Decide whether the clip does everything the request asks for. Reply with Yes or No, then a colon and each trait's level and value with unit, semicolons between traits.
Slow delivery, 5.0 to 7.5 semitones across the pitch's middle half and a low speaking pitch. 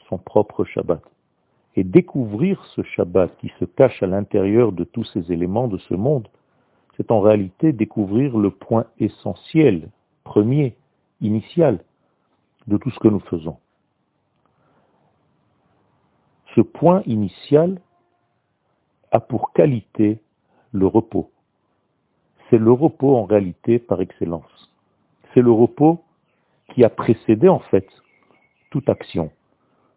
Yes: slow, 120 wpm; average, 5.3 semitones; low, 115 Hz